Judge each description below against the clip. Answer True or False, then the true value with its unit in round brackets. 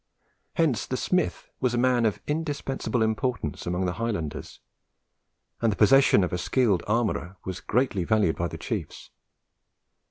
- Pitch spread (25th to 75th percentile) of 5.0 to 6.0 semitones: True (5.5 semitones)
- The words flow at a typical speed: True (150 wpm)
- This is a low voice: True (110 Hz)